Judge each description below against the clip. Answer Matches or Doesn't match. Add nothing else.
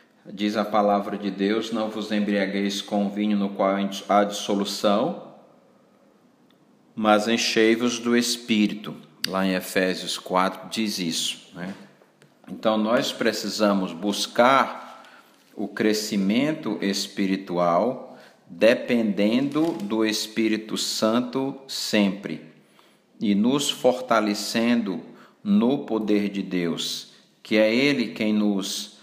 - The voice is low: Matches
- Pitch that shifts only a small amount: Matches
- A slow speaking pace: Matches